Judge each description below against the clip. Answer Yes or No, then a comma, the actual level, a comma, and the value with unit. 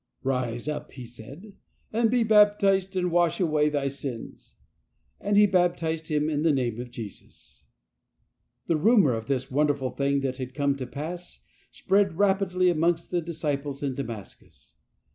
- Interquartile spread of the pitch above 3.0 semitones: Yes, average, 5.2 semitones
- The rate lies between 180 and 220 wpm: No, average, 160 wpm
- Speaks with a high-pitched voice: No, medium, 150 Hz